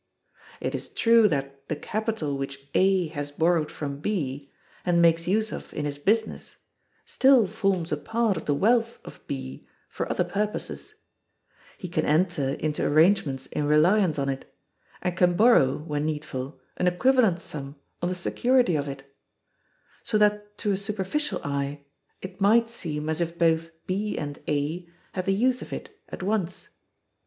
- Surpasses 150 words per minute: Yes, average, 165 wpm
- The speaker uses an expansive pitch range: Yes, wide, 6.0 semitones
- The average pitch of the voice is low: No, medium, 170 Hz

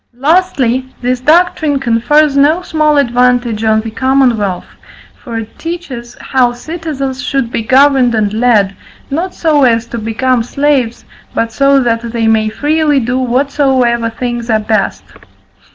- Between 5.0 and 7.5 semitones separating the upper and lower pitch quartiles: No, average, 3.7 semitones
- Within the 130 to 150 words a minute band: Yes, average, 140 wpm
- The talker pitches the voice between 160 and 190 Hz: No, very high, 250 Hz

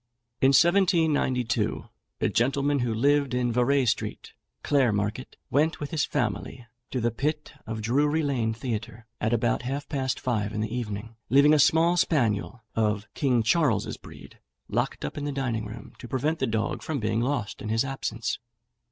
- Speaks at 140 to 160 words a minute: No, average, 170 wpm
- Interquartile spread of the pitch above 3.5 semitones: Yes, average, 4.3 semitones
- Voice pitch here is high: No, low, 125 Hz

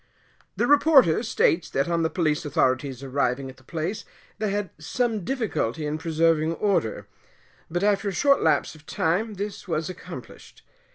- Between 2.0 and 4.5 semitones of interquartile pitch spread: No, wide, 5.4 semitones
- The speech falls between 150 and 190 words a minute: Yes, average, 160 wpm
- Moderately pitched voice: Yes, medium, 165 Hz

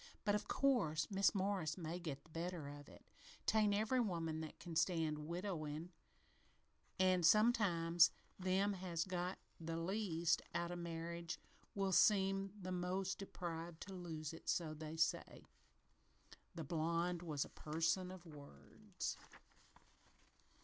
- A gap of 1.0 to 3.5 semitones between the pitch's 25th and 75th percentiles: Yes, average, 2.8 semitones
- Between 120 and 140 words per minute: Yes, slow, 135 wpm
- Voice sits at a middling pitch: Yes, medium, 170 Hz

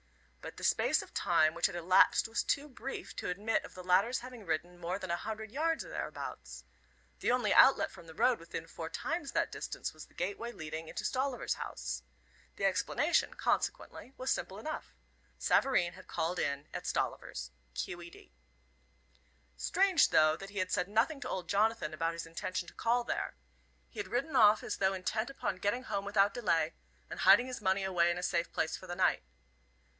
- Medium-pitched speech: No, high, 195 Hz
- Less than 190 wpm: No, average, 195 wpm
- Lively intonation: Yes, wide, 6.1 semitones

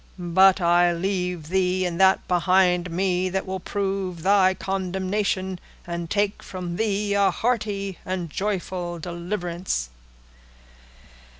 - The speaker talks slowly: Yes, slow, 115 wpm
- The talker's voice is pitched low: No, medium, 185 Hz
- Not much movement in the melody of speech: Yes, narrow, 1.7 semitones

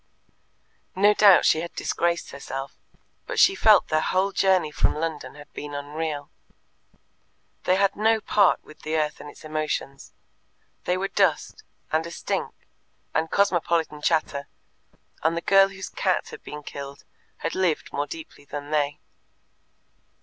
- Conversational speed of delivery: Yes, average, 150 wpm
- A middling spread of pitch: Yes, average, 4.3 semitones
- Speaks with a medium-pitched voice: Yes, medium, 160 Hz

